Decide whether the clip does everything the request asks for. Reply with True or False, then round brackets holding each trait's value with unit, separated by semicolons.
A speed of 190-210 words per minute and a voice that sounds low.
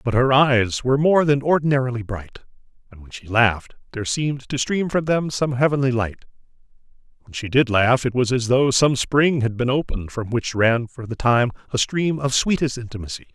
True (200 wpm; 125 Hz)